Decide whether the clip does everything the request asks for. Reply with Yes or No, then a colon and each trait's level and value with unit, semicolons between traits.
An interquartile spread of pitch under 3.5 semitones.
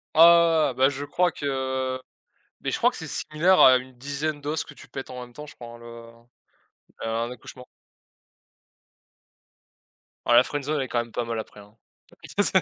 No: average, 3.9 semitones